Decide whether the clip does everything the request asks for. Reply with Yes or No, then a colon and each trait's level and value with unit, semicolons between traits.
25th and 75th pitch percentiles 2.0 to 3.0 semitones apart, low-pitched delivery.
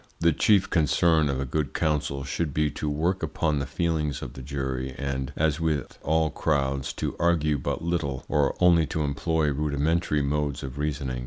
Yes: narrow, 2.6 semitones; very low, 75 Hz